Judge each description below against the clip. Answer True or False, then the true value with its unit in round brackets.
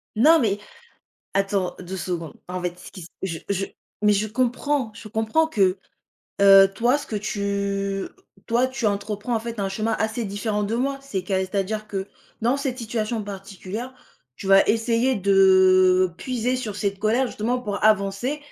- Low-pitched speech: False (210 Hz)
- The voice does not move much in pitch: False (3.3 semitones)